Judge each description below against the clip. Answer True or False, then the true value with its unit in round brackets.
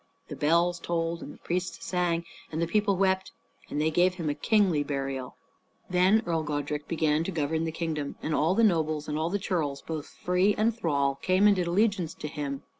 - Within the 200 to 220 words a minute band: True (205 wpm)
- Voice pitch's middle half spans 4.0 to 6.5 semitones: False (3.5 semitones)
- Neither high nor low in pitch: True (165 Hz)